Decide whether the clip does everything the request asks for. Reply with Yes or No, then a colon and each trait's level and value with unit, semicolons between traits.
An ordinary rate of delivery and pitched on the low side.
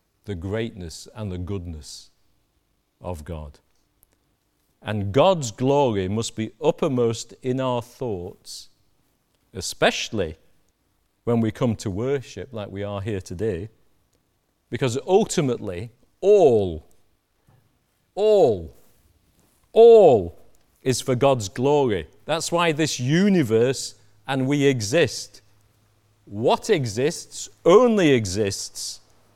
No: slow, 95 wpm; low, 110 Hz